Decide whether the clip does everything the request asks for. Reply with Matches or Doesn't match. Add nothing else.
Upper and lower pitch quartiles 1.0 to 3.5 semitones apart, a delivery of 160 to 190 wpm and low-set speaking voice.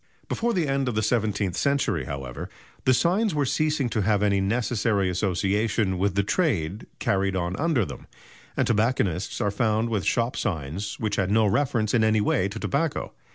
Doesn't match